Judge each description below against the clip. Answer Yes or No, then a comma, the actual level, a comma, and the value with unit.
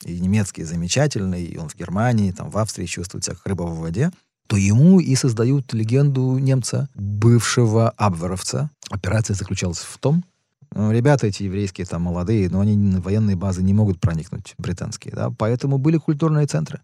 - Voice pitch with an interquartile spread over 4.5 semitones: Yes, wide, 5.6 semitones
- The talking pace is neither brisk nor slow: No, fast, 170 wpm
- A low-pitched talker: Yes, low, 110 Hz